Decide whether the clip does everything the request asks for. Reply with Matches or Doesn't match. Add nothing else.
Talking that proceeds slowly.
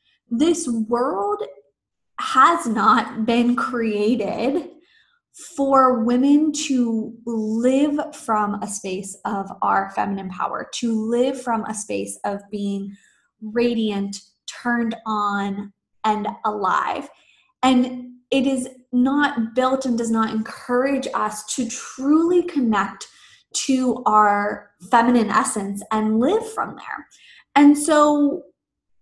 Matches